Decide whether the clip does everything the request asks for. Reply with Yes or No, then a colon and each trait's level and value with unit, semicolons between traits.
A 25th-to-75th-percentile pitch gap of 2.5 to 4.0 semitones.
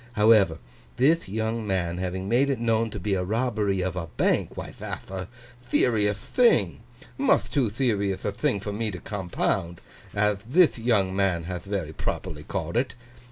Yes: average, 3.6 semitones